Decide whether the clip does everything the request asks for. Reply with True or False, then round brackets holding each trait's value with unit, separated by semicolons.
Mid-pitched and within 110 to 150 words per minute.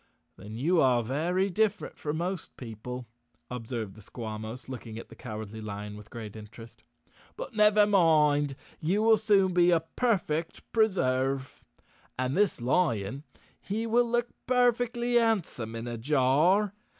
True (150 Hz; 140 wpm)